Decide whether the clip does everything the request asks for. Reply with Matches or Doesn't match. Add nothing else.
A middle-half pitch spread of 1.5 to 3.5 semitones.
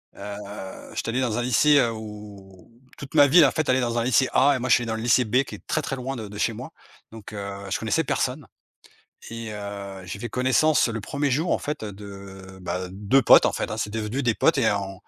Doesn't match